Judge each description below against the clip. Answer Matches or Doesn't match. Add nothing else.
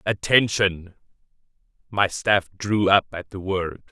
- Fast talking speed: Doesn't match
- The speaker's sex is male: Matches